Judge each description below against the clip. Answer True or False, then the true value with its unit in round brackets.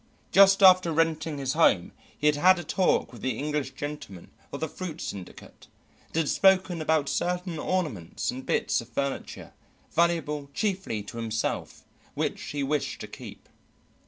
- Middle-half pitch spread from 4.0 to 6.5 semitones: True (4.9 semitones)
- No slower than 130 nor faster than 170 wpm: True (160 wpm)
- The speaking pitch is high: False (150 Hz)